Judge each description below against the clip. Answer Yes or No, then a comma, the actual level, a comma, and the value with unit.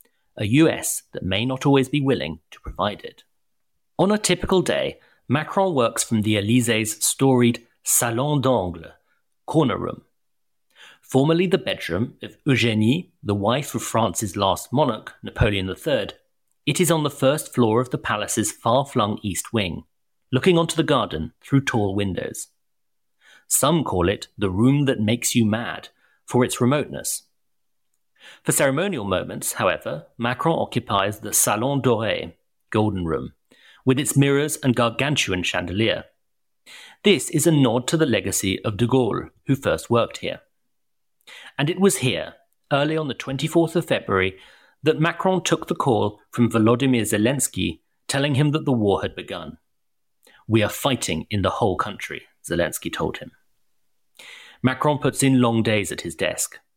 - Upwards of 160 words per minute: No, average, 150 wpm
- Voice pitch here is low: Yes, low, 125 Hz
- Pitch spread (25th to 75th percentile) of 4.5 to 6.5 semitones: Yes, average, 5.0 semitones